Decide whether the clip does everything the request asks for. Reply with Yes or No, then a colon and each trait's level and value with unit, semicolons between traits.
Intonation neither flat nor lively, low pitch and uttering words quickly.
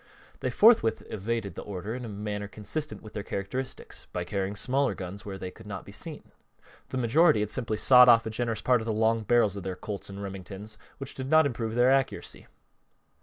Yes: average, 3.8 semitones; low, 110 Hz; fast, 210 wpm